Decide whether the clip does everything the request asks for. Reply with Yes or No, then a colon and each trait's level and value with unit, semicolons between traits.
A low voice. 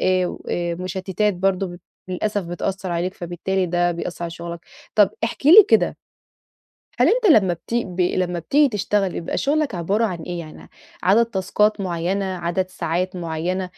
No: medium, 185 Hz